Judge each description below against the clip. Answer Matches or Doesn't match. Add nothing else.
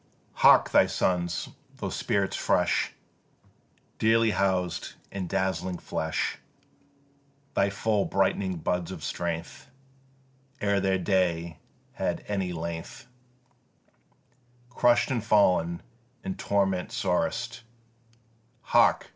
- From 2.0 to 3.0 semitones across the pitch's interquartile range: Matches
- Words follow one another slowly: Matches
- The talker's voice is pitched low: Matches